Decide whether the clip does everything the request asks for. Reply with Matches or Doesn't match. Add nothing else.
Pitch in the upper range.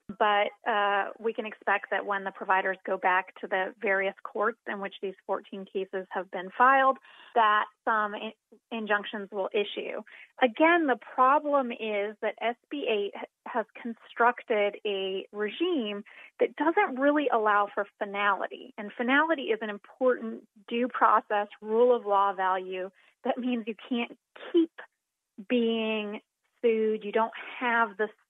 Matches